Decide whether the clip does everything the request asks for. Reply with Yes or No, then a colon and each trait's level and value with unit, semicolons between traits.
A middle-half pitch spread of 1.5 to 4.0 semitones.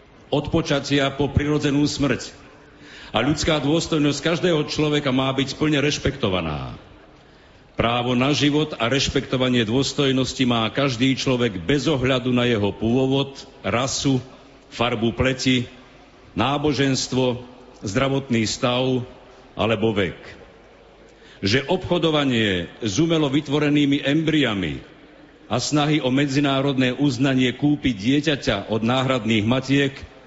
Yes: average, 2.7 semitones